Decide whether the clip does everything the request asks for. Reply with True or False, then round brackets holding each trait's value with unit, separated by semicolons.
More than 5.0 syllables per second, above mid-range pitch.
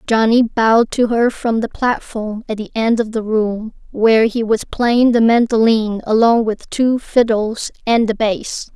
False (4.2 syllables/s; 225 Hz)